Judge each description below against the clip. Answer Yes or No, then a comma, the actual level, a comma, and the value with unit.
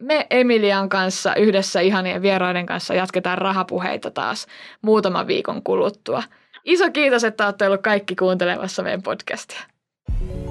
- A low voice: No, high, 195 Hz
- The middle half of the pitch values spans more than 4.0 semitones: No, average, 3.3 semitones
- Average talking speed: Yes, average, 125 wpm